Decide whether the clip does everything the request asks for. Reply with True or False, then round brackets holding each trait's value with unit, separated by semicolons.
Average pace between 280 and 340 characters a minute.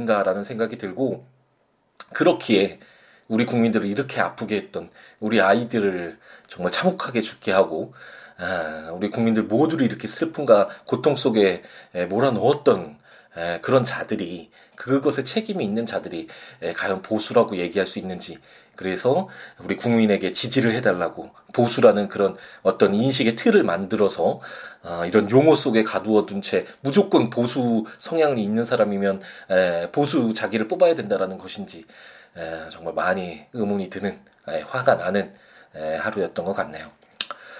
True (310 characters per minute)